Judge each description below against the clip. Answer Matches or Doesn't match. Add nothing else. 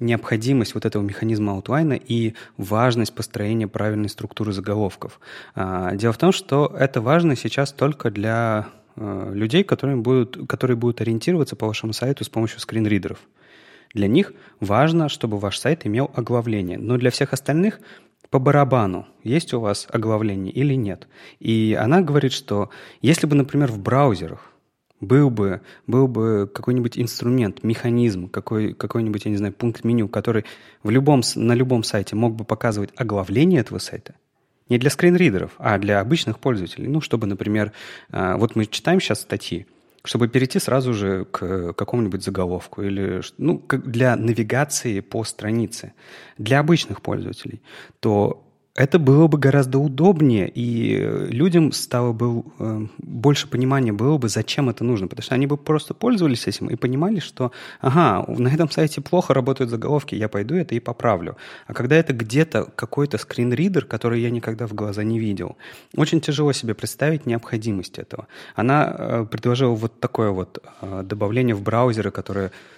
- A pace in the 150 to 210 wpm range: Matches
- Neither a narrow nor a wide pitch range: Matches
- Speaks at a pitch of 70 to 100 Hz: Doesn't match